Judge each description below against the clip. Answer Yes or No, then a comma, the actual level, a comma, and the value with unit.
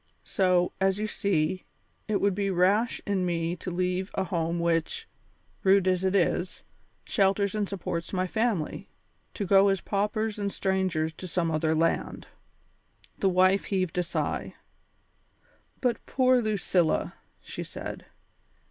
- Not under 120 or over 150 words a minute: Yes, average, 140 wpm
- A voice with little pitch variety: Yes, narrow, 2.3 semitones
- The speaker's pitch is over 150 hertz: Yes, high, 190 Hz